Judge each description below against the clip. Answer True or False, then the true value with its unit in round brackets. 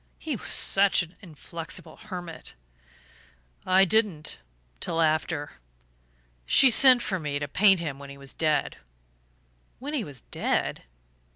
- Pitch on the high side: False (170 Hz)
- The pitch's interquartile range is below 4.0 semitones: False (5.3 semitones)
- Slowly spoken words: True (130 wpm)